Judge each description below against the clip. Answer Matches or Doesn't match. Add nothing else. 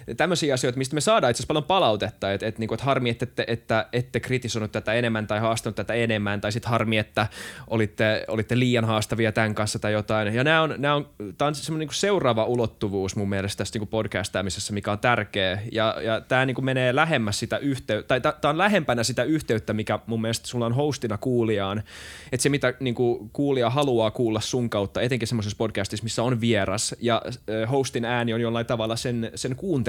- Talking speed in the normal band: Doesn't match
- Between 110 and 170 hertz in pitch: Matches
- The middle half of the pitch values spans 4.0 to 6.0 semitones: Doesn't match